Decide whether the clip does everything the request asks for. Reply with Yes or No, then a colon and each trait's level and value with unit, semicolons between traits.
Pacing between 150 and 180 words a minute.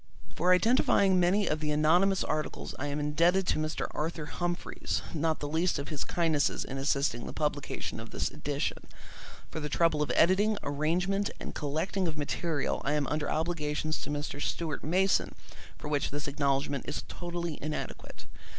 Yes: average, 170 wpm